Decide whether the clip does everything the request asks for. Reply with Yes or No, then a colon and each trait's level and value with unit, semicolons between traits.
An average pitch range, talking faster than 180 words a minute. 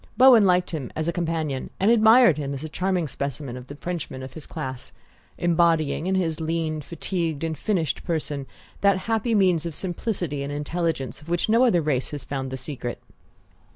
Yes: average, 4.2 semitones; average, 190 wpm